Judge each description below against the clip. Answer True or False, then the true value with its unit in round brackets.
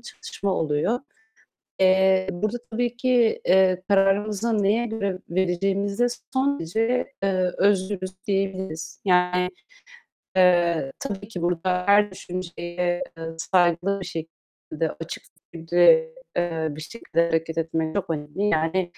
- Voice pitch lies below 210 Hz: True (185 Hz)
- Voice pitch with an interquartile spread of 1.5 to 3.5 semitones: True (2.9 semitones)